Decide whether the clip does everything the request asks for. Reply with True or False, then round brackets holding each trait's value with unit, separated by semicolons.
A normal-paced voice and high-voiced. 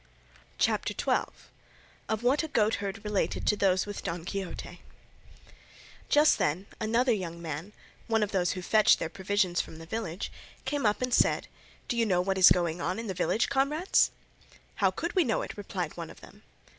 True (180 wpm; 200 Hz)